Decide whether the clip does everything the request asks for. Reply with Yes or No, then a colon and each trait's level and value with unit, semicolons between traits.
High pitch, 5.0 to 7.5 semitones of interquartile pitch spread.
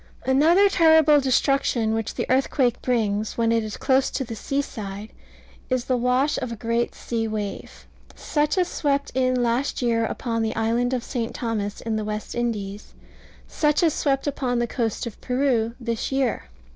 No: high, 240 Hz; average, 3.3 semitones